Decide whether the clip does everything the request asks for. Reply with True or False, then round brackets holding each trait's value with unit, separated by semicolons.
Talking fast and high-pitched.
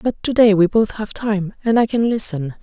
True (250 wpm; 210 Hz)